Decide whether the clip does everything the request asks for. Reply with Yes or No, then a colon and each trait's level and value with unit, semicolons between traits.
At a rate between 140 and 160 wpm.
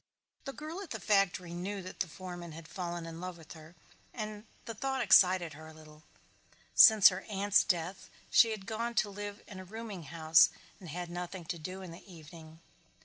No: average, 195 wpm